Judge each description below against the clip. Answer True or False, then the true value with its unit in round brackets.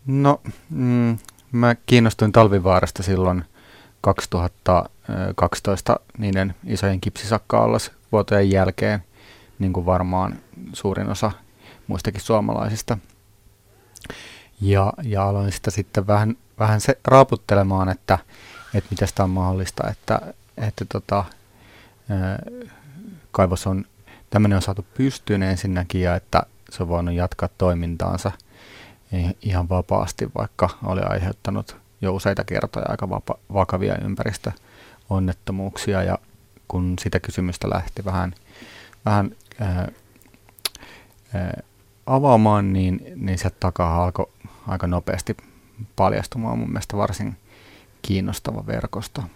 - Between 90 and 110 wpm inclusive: True (105 wpm)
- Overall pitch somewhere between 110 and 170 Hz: False (100 Hz)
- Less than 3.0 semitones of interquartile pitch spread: True (2.6 semitones)